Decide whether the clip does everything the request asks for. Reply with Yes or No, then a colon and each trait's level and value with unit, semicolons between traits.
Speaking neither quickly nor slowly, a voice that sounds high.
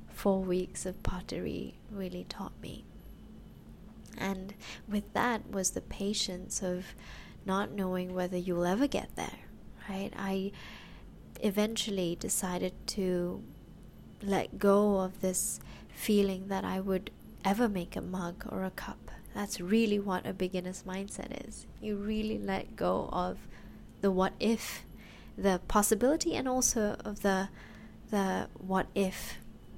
No: slow, 130 wpm; high, 195 Hz